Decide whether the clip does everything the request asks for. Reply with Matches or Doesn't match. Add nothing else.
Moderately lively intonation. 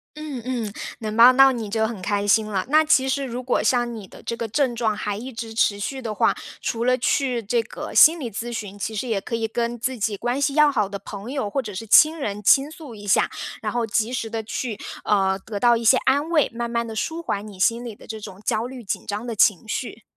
Matches